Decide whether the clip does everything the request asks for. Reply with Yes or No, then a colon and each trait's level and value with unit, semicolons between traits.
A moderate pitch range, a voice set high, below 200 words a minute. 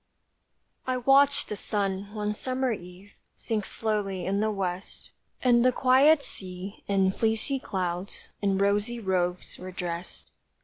Yes: average, 4.1 semitones; high, 205 Hz; slow, 135 wpm